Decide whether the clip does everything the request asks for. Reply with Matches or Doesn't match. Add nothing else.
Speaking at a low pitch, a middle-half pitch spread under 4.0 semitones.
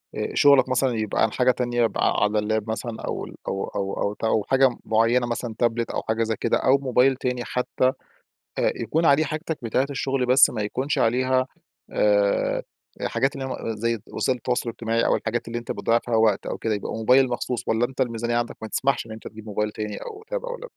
Matches